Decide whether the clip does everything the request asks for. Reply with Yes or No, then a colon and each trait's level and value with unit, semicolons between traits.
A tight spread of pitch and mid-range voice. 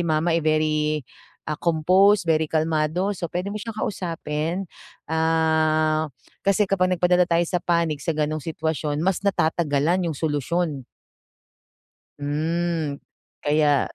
Yes: narrow, 2.3 semitones; medium, 160 Hz